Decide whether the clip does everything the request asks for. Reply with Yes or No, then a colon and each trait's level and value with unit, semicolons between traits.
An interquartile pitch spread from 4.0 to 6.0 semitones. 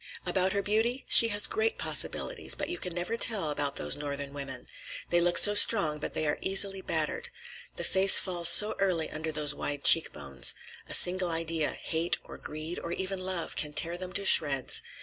Yes: average, 4.4 semitones